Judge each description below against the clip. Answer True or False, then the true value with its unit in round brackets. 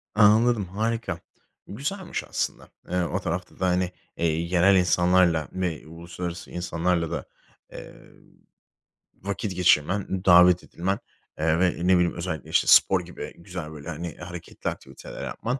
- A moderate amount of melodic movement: False (2.1 semitones)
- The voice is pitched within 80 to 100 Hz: True (90 Hz)